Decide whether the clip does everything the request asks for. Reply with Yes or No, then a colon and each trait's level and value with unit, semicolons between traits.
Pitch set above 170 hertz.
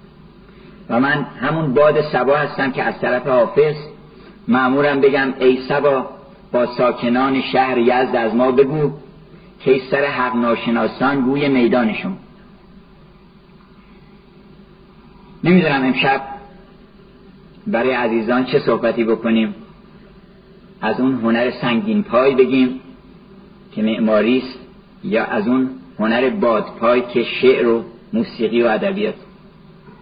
Yes: medium, 185 Hz